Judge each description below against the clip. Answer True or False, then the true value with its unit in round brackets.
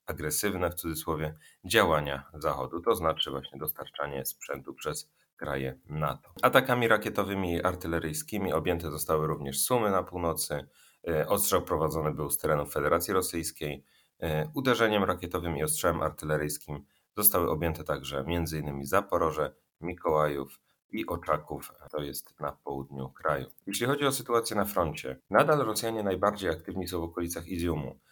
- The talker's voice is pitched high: False (80 Hz)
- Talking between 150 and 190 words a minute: False (135 wpm)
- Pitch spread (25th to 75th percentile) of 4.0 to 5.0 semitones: True (4.3 semitones)